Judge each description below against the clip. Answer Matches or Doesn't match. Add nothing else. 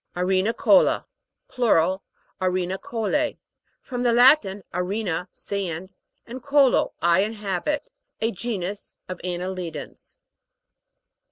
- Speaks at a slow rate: Matches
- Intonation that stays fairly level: Doesn't match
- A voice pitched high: Matches